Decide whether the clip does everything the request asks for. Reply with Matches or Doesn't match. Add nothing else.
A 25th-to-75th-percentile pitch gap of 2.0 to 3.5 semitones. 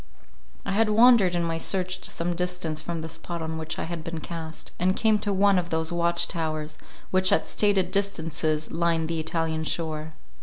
Matches